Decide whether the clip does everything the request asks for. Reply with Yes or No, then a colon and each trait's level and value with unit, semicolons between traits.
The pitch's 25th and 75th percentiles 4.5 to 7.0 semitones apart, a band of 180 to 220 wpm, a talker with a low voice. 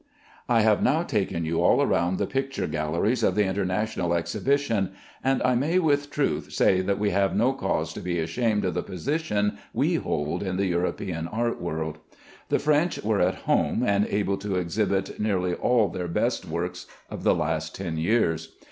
Yes: average, 5.2 semitones; average, 185 wpm; low, 100 Hz